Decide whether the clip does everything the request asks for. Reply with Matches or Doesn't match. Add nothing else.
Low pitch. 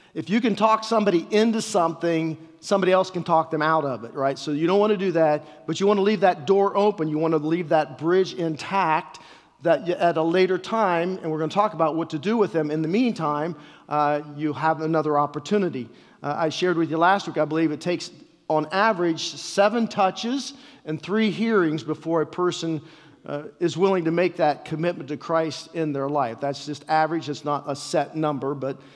Doesn't match